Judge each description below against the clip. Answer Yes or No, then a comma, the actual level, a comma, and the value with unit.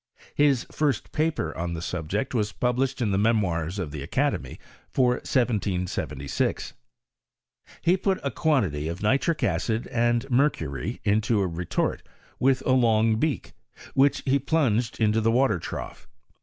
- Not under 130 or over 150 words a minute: Yes, average, 145 wpm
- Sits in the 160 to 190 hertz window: No, low, 115 Hz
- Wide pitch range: Yes, wide, 6.7 semitones